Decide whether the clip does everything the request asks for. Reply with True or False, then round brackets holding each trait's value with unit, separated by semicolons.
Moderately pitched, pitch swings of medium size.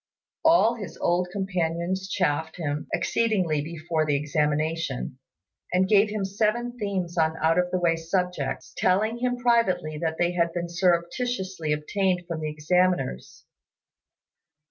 True (175 Hz; 3.4 semitones)